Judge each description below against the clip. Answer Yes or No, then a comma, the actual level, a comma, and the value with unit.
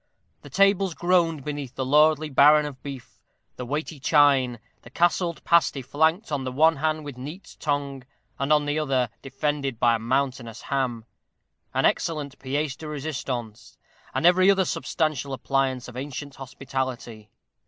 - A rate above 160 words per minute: No, average, 155 wpm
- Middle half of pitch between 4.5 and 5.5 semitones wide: No, average, 3.0 semitones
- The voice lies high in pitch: No, medium, 140 Hz